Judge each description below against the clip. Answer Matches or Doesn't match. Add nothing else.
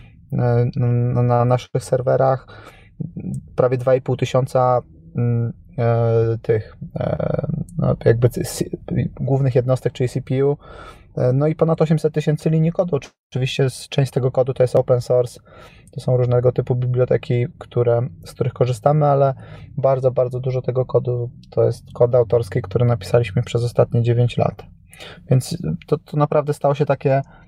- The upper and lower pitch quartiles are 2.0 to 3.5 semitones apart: Matches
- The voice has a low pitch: Matches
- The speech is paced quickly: Doesn't match